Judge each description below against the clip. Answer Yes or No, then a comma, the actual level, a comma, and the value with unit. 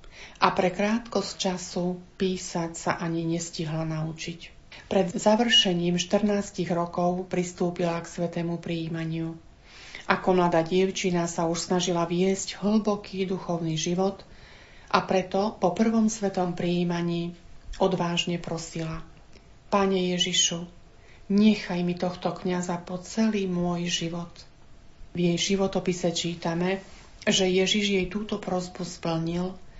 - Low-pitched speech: No, medium, 180 Hz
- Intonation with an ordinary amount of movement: No, narrow, 2.0 semitones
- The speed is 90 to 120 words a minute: Yes, slow, 110 wpm